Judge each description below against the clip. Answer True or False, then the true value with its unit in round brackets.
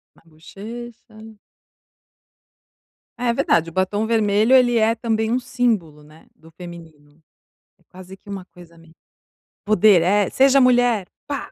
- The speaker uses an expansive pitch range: True (5.8 semitones)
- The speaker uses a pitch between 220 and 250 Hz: False (205 Hz)